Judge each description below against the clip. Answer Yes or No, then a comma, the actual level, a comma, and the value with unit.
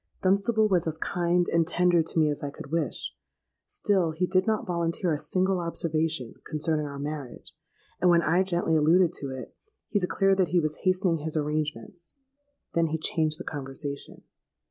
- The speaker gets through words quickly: No, average, 175 wpm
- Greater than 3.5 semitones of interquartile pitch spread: No, average, 2.9 semitones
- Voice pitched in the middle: Yes, medium, 165 Hz